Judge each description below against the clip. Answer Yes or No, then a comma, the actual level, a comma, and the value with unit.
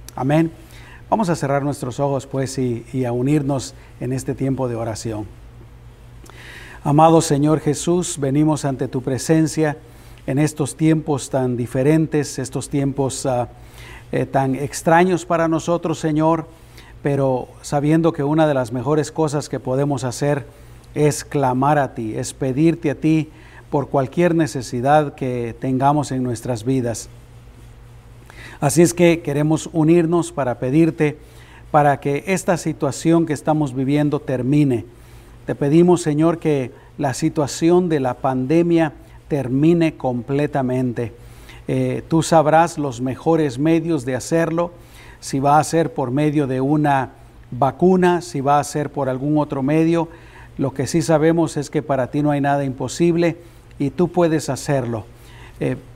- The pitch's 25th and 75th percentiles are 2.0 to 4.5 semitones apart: Yes, average, 3.7 semitones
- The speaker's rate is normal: Yes, average, 140 wpm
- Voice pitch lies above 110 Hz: Yes, medium, 140 Hz